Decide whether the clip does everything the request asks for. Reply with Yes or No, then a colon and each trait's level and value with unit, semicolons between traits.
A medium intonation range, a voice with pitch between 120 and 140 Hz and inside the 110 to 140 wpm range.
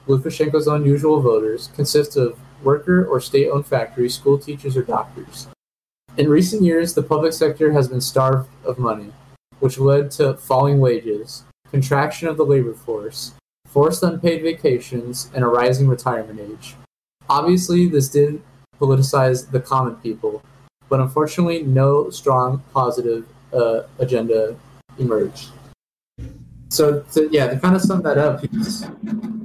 Yes: average, 3.1 semitones; low, 135 Hz; slow, 135 wpm